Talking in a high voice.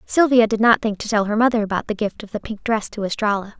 Yes: high, 215 Hz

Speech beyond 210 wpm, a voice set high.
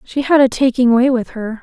Yes: fast, 260 wpm; very high, 250 Hz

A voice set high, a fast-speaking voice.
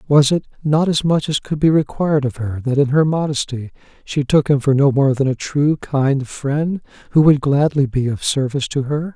No: medium, 140 Hz; fast, 225 wpm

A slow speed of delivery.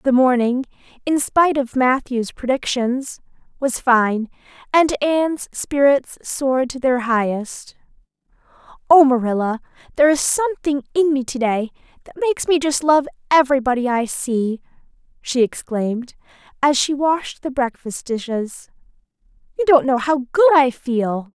Yes: slow, 130 wpm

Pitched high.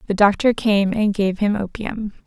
Yes: high, 205 Hz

